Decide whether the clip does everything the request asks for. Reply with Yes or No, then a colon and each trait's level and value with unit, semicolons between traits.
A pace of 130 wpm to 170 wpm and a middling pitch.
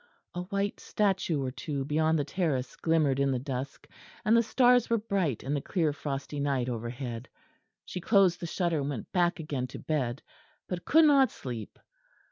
No: average, 180 wpm; medium, 155 Hz